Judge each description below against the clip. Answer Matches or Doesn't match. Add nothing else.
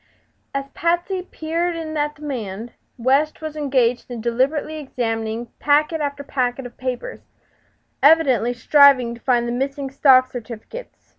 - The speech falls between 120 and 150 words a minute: Matches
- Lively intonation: Doesn't match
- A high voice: Matches